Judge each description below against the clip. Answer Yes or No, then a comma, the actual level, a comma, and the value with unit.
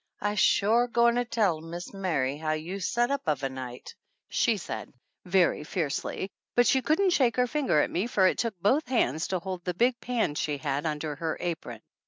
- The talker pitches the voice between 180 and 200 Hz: Yes, medium, 185 Hz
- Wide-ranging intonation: Yes, wide, 7.3 semitones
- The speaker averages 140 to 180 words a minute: No, fast, 205 wpm